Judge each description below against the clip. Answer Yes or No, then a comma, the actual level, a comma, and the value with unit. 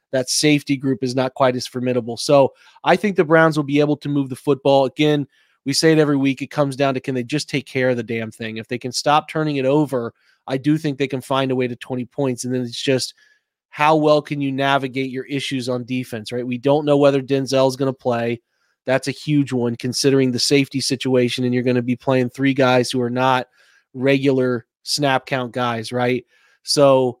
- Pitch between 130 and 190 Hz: Yes, low, 135 Hz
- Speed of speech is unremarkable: No, fast, 230 wpm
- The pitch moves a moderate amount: No, narrow, 2.1 semitones